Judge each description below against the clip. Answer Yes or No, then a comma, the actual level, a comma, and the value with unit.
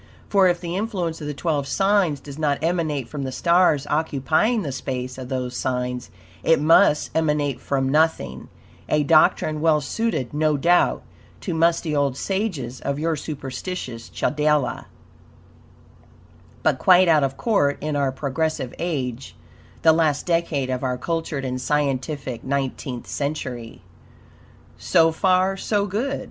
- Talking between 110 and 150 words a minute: Yes, average, 140 wpm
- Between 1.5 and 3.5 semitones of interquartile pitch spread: No, average, 4.0 semitones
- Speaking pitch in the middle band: Yes, medium, 150 Hz